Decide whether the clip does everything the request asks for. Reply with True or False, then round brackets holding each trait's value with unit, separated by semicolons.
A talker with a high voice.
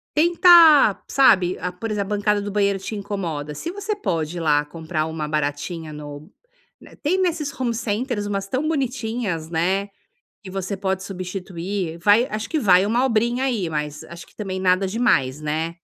True (195 Hz)